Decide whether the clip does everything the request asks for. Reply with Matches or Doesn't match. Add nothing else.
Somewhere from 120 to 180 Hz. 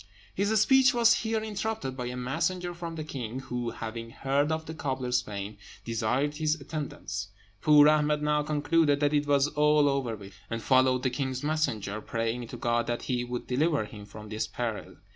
Matches